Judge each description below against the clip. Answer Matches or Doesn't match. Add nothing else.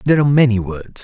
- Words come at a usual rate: Doesn't match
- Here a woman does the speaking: Doesn't match